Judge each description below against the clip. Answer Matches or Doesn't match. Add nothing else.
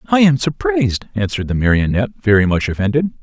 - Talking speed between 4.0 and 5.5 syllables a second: Doesn't match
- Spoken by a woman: Doesn't match